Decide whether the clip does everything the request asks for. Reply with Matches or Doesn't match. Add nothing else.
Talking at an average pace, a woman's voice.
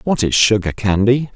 Doesn't match